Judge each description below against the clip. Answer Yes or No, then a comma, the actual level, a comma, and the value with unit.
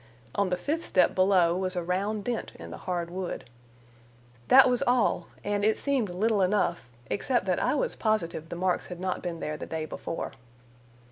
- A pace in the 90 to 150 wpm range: No, average, 190 wpm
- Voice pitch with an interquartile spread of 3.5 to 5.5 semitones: Yes, average, 3.9 semitones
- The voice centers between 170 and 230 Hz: Yes, medium, 185 Hz